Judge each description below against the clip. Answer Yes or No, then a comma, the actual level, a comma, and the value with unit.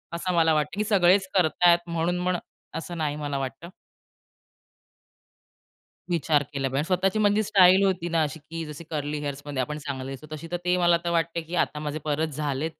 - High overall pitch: No, medium, 160 Hz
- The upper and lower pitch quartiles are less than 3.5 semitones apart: Yes, average, 3.1 semitones